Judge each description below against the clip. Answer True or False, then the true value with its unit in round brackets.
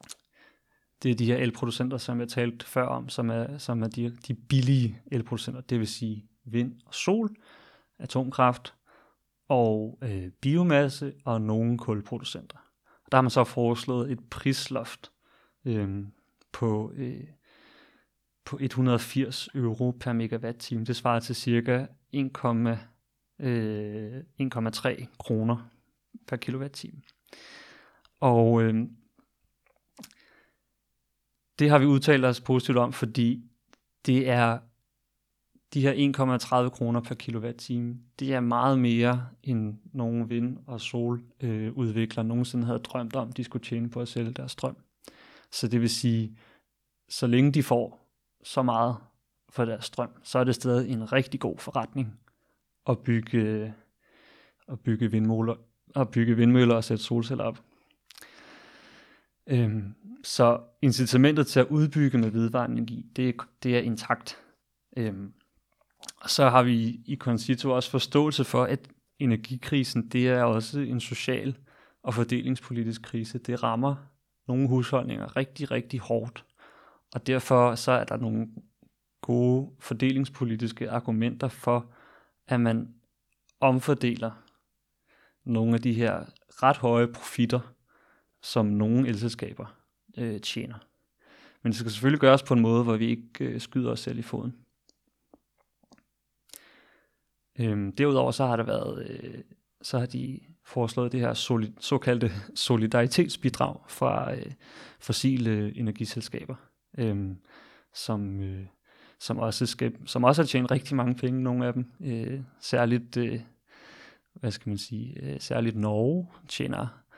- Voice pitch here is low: True (120 Hz)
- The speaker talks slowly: True (130 wpm)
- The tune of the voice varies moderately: False (2.0 semitones)